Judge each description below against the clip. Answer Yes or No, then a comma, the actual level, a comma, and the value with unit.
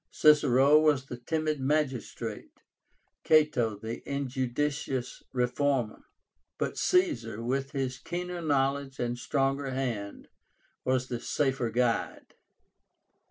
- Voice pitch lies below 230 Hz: Yes, low, 135 Hz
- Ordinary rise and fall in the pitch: Yes, average, 3.2 semitones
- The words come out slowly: Yes, slow, 100 wpm